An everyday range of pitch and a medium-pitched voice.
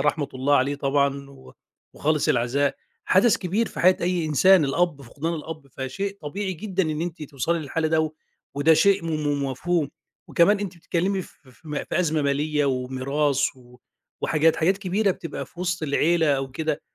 Yes: average, 4.0 semitones; medium, 155 Hz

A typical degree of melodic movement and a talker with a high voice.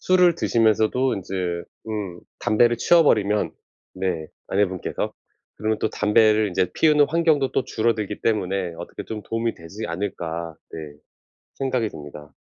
No: average, 4.3 semitones; low, 105 Hz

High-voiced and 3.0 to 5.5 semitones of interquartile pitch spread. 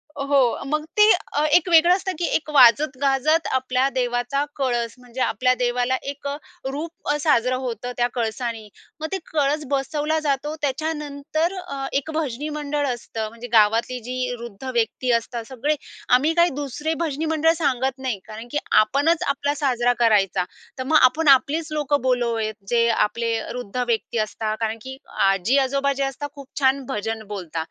Yes: very high, 260 Hz; average, 3.6 semitones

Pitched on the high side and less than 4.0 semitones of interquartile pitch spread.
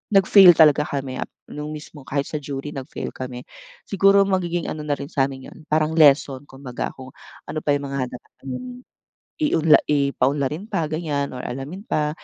No: medium, 150 Hz; average, 2.9 semitones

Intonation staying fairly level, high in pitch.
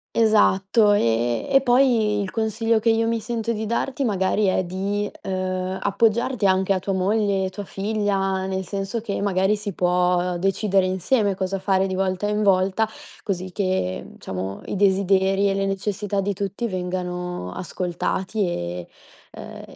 Yes: narrow, 2.1 semitones; high, 195 Hz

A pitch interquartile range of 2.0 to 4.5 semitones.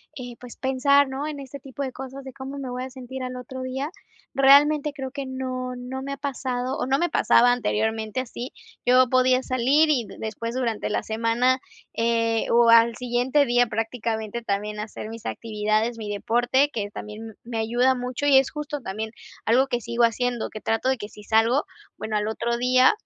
Yes: narrow, 2.6 semitones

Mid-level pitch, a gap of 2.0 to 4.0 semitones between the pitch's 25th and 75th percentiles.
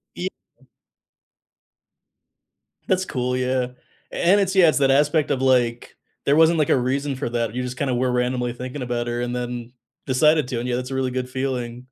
No: low, 130 Hz; narrow, 2.4 semitones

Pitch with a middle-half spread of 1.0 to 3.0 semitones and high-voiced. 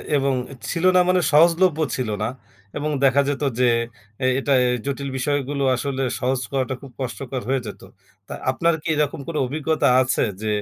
No: narrow, 2.6 semitones; medium, 140 Hz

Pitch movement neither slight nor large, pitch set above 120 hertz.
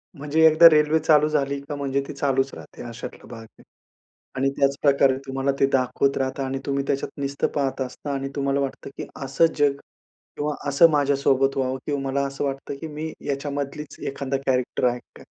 No: narrow, 1.2 semitones; medium, 140 Hz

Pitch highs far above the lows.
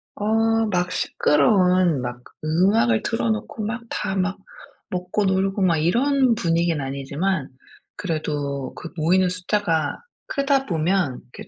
No: average, 5.0 semitones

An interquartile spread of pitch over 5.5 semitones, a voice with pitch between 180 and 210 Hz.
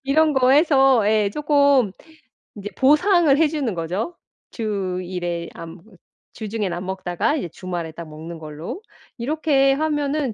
No: wide, 8.4 semitones; high, 225 Hz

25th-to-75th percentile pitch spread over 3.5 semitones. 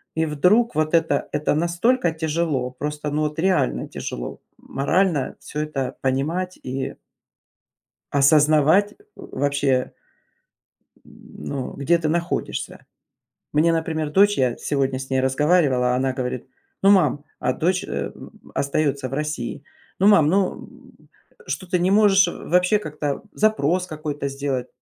Yes: average, 4.2 semitones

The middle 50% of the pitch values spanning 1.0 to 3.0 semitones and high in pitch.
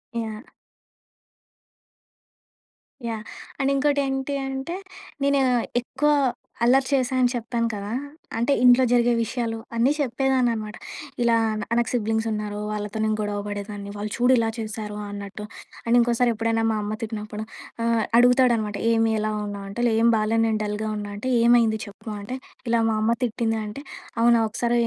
Yes: narrow, 2.4 semitones; high, 225 Hz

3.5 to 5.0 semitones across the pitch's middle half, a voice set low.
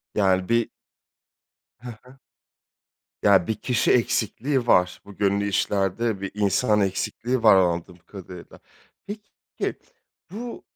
Yes: average, 4.0 semitones; low, 100 Hz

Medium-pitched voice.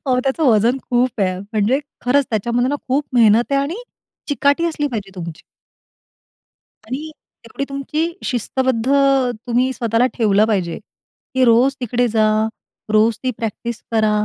No: high, 245 Hz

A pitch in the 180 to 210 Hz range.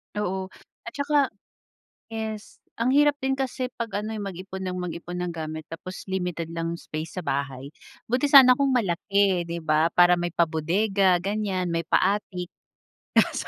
Yes: medium, 185 Hz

